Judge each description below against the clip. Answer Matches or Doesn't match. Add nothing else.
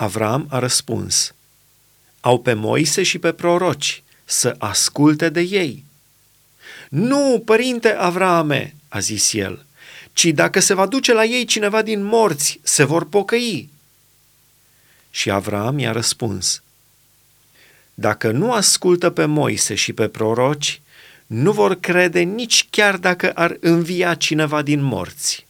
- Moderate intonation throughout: Doesn't match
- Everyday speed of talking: Matches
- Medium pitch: Matches